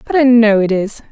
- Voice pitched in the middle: No, high, 225 Hz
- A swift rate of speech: Yes, fast, 270 wpm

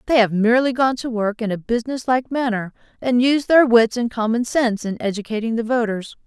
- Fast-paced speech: Yes, fast, 210 wpm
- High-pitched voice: Yes, high, 235 Hz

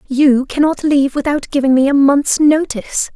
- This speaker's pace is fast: No, average, 190 wpm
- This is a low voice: No, very high, 280 Hz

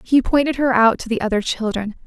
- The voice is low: No, high, 235 Hz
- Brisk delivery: Yes, fast, 230 wpm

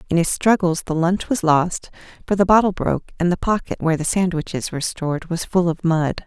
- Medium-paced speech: No, fast, 220 wpm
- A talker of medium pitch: Yes, medium, 175 Hz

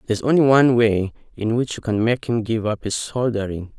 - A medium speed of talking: No, fast, 240 wpm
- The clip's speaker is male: Yes, male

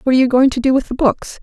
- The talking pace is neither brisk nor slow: No, fast, 380 wpm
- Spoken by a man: No, female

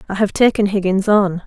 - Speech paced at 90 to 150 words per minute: No, fast, 205 wpm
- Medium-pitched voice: No, high, 200 Hz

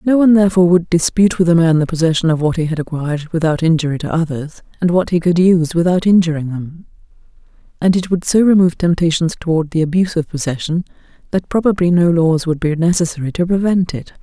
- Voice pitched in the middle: Yes, medium, 170 Hz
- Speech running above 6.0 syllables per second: Yes, 6.5 syllables/s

